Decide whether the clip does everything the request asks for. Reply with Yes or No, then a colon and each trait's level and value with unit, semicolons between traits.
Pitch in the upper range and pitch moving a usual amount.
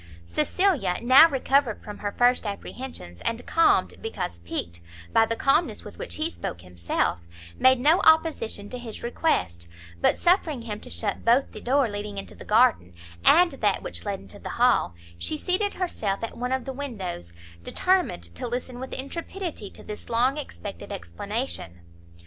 No: high, 240 Hz; wide, 5.9 semitones